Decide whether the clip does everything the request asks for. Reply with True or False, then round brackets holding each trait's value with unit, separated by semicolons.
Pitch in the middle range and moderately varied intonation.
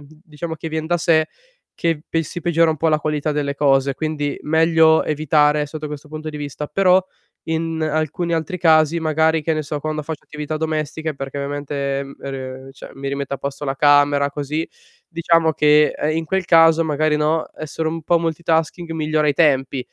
False (155 Hz; 2.0 semitones)